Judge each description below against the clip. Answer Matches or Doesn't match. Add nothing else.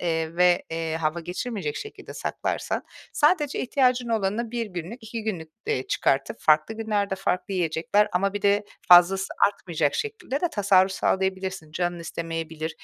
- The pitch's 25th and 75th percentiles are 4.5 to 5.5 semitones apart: Matches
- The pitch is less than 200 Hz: Matches